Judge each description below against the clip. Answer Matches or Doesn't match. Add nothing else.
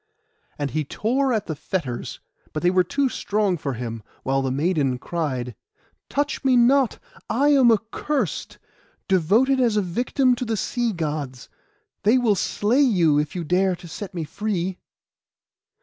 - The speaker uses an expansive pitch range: Matches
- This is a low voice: Doesn't match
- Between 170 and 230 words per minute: Doesn't match